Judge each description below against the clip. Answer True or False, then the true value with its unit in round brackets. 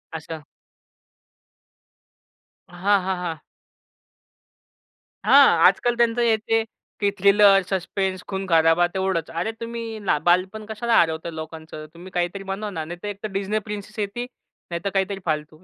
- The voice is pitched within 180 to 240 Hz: True (190 Hz)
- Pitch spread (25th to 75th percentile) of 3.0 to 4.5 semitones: True (3.7 semitones)